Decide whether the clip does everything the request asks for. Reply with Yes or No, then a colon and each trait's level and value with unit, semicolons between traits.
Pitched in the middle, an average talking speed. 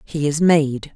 Yes: medium, 150 Hz; average, 190 wpm